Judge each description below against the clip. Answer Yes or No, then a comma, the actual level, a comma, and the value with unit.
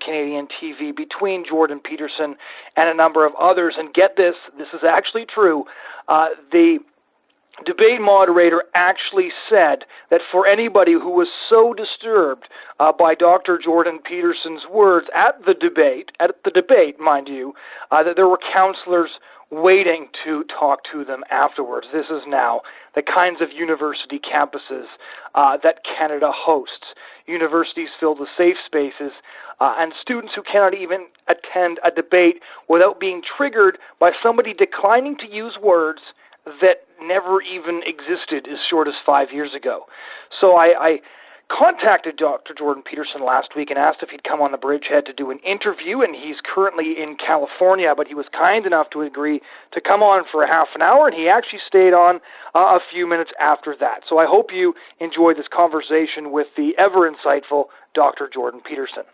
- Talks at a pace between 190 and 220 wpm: No, average, 170 wpm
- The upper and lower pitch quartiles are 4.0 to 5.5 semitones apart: Yes, average, 4.5 semitones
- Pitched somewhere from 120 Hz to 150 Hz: No, medium, 170 Hz